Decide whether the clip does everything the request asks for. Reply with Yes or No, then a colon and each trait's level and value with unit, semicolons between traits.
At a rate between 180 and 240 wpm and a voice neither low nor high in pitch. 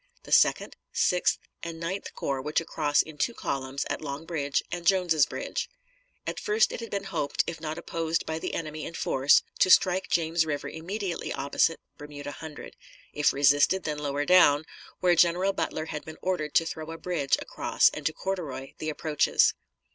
Yes: average, 185 wpm; medium, 160 Hz